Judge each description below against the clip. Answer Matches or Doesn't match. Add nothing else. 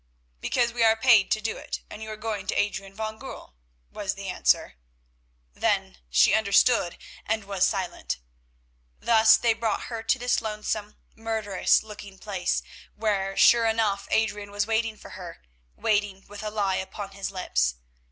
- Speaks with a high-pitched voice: Matches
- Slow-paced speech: Doesn't match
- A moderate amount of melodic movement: Doesn't match